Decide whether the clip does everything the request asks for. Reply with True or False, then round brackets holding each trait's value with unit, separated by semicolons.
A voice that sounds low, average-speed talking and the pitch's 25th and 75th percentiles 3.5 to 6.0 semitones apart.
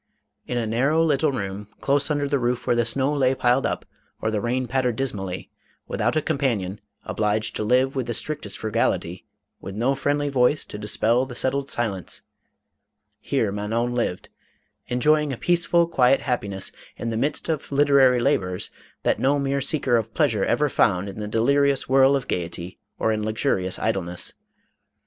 True (125 Hz; 170 wpm; 4.5 semitones)